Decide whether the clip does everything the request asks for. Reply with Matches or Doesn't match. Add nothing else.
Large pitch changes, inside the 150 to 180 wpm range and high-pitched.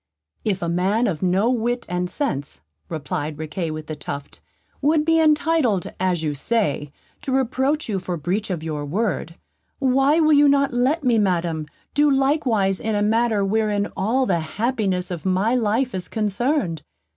Matches